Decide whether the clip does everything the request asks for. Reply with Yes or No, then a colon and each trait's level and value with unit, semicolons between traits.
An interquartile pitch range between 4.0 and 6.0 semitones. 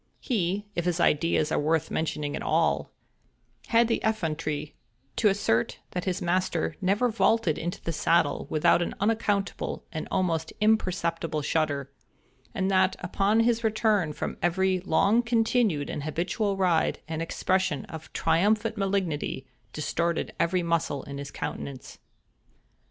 Yes: average, 4.3 semitones